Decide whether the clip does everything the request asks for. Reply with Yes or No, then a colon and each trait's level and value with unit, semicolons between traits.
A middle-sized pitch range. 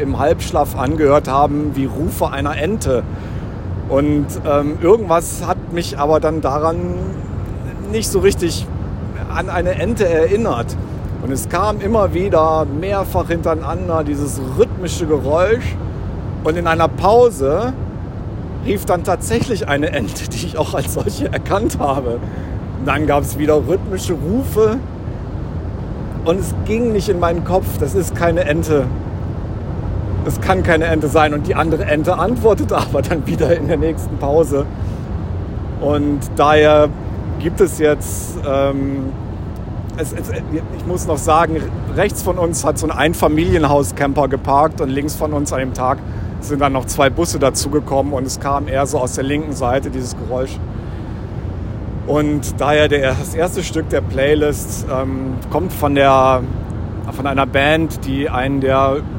No: wide, 6.1 semitones